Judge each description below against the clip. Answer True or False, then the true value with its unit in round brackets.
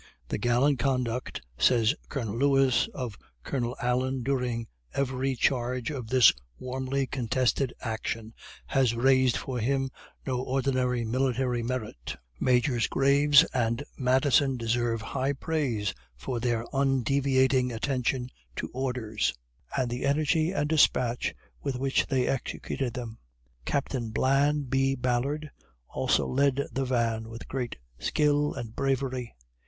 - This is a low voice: True (130 Hz)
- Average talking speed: False (125 wpm)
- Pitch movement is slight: True (2.2 semitones)